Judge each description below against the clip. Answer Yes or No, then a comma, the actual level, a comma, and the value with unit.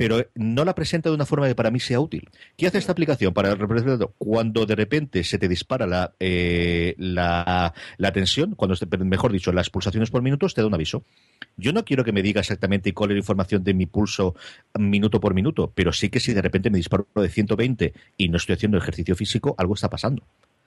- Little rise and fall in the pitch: No, average, 4.2 semitones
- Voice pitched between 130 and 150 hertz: No, low, 105 Hz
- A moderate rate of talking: No, fast, 225 wpm